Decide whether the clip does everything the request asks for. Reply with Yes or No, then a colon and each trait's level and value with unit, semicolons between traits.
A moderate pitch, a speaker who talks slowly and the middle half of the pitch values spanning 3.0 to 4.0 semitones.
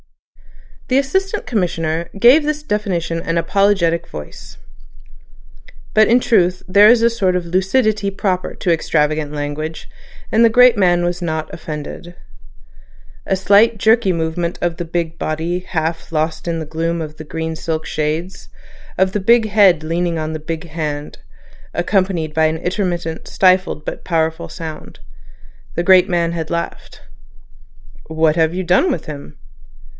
No: medium, 170 Hz; average, 150 wpm; average, 3.5 semitones